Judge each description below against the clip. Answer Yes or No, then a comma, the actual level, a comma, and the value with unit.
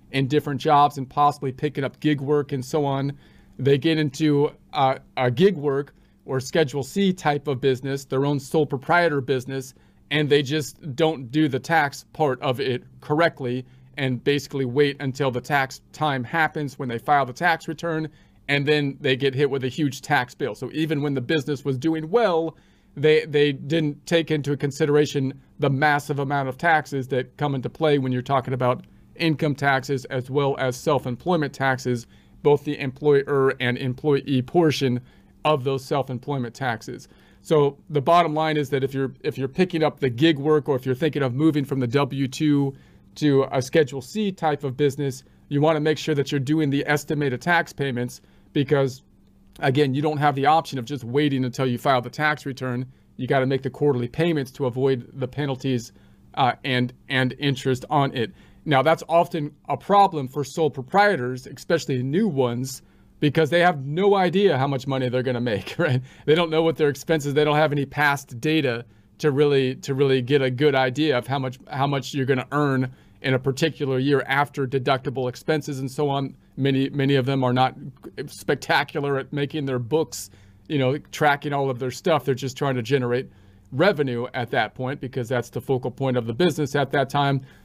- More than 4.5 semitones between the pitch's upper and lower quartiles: No, narrow, 2.4 semitones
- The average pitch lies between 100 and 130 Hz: No, medium, 140 Hz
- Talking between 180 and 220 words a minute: Yes, average, 195 wpm